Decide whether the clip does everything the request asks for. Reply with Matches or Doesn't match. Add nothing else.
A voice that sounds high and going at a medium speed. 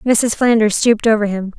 Matches